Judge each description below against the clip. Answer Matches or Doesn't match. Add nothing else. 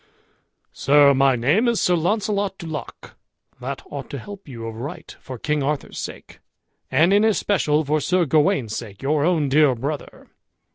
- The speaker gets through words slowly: Doesn't match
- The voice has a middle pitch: Matches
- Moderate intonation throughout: Matches